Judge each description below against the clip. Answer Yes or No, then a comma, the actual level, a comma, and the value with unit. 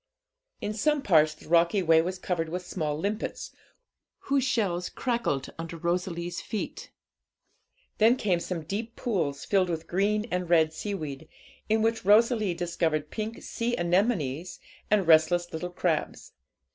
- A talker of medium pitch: Yes, medium, 180 Hz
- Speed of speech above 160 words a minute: No, average, 140 wpm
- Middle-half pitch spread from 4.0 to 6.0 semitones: Yes, average, 4.4 semitones